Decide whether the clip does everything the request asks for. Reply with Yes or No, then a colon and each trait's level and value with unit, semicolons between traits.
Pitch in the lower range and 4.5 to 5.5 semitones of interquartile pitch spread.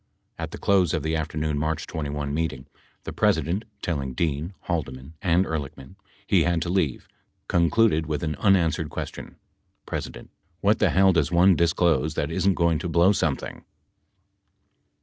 No: very low, 80 Hz; average, 2.9 semitones